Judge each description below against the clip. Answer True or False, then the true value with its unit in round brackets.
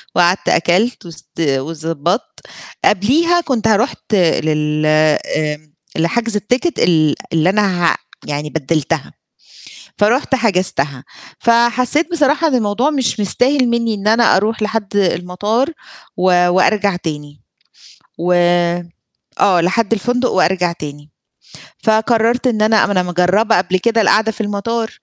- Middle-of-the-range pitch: False (205 Hz)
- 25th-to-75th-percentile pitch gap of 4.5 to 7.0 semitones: True (5.5 semitones)